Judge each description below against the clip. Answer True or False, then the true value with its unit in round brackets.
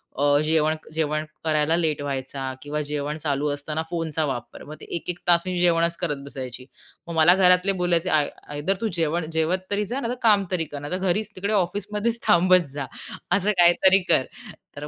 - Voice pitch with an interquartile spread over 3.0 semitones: True (3.7 semitones)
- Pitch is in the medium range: True (165 Hz)